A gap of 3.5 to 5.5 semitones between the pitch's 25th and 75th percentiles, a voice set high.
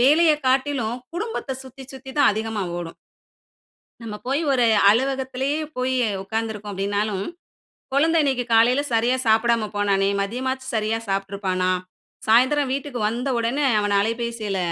Yes: average, 4.0 semitones; high, 235 Hz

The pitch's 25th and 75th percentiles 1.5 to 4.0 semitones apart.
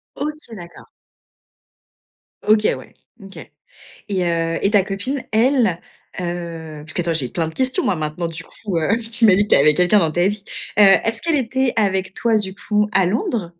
No: average, 4.8 semitones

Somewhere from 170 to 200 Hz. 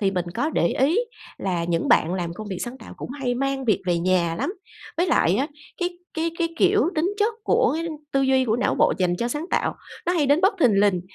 No: very high, 255 Hz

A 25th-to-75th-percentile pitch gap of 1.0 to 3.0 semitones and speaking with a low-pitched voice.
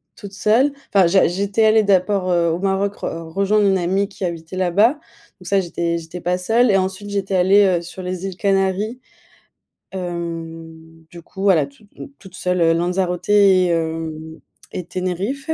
No: average, 2.7 semitones; medium, 185 Hz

